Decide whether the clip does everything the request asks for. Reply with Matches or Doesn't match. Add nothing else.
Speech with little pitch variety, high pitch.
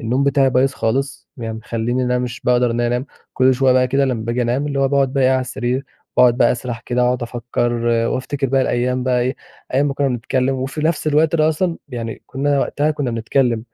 Doesn't match